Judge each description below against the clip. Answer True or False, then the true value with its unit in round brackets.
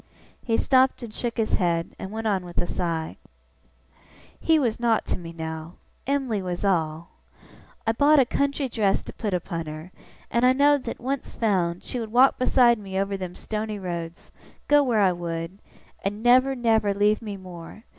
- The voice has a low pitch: False (210 Hz)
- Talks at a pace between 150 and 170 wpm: False (185 wpm)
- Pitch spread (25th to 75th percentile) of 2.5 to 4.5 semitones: False (5.6 semitones)